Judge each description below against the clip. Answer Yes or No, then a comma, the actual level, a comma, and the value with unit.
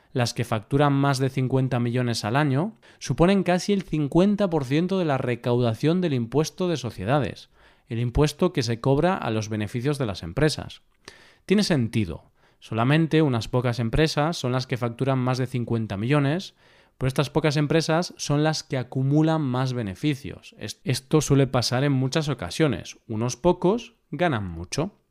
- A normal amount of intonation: Yes, average, 4.5 semitones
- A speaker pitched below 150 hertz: Yes, medium, 140 Hz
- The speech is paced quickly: No, average, 155 wpm